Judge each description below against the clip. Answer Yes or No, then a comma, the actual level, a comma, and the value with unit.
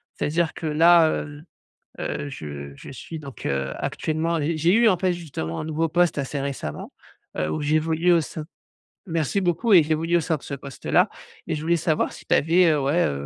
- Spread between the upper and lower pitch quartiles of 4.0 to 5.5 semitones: No, average, 3.2 semitones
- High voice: No, medium, 155 Hz